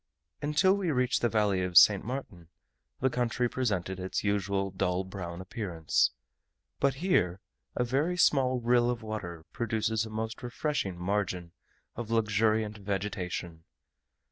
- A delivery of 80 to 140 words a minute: Yes, slow, 135 wpm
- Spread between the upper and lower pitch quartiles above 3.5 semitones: Yes, average, 4.7 semitones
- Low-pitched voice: Yes, low, 110 Hz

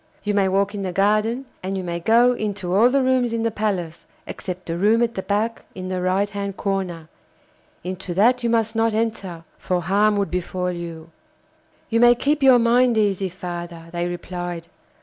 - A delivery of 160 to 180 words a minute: No, average, 190 wpm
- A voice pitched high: Yes, high, 200 Hz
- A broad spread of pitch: No, average, 4.0 semitones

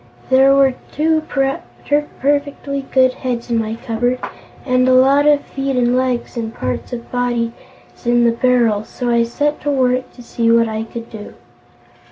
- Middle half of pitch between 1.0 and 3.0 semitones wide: Yes, average, 2.7 semitones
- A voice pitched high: Yes, very high, 250 Hz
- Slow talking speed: No, average, 170 wpm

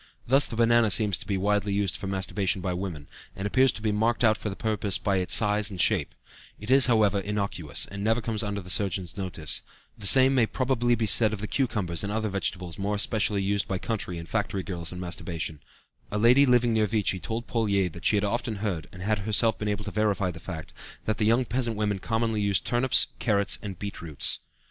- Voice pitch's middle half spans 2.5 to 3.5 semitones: Yes, average, 2.8 semitones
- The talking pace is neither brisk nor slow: No, fast, 225 wpm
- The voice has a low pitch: Yes, low, 105 Hz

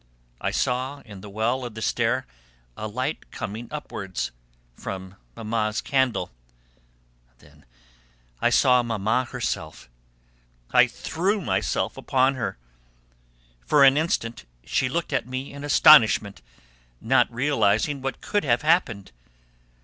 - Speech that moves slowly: Yes, slow, 120 wpm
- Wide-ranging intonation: No, average, 4.3 semitones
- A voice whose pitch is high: No, low, 125 Hz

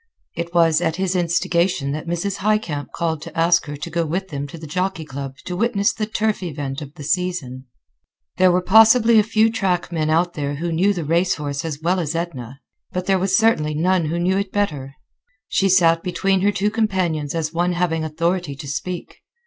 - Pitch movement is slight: No, average, 3.6 semitones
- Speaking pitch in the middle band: Yes, medium, 170 Hz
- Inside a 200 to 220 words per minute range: Yes, fast, 205 wpm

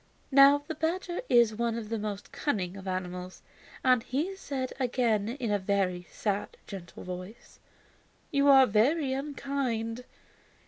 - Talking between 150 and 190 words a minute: No, average, 140 wpm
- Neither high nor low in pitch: No, high, 235 Hz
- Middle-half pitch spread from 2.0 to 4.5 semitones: No, wide, 5.5 semitones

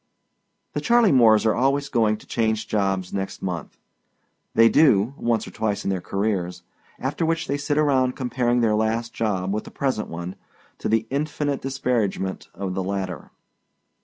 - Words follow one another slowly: No, average, 165 wpm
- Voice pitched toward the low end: Yes, low, 110 Hz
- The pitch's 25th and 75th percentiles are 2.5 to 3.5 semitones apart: No, average, 5.2 semitones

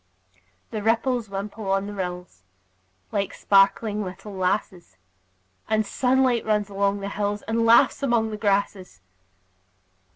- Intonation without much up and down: Yes, narrow, 2.2 semitones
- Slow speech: Yes, slow, 125 wpm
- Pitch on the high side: Yes, high, 205 Hz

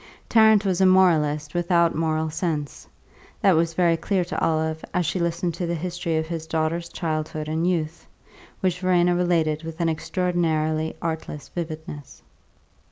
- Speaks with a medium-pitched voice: Yes, medium, 165 Hz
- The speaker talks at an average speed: Yes, average, 155 wpm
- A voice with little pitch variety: Yes, narrow, 2.0 semitones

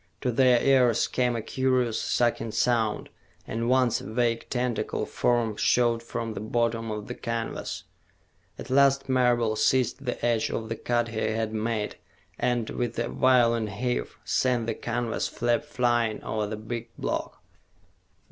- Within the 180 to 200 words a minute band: No, average, 155 wpm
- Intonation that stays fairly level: Yes, narrow, 1.6 semitones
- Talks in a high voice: No, low, 120 Hz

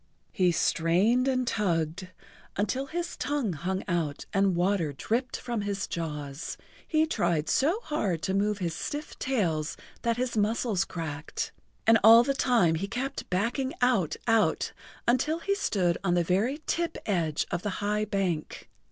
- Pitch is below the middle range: No, high, 205 Hz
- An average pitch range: No, wide, 6.4 semitones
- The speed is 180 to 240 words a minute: No, average, 155 wpm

